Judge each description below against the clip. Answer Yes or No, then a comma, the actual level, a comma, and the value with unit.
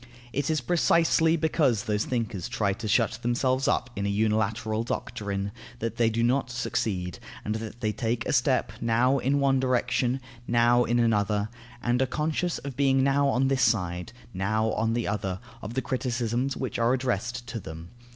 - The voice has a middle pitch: No, low, 120 Hz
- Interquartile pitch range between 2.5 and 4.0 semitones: Yes, average, 3.3 semitones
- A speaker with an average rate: Yes, average, 180 wpm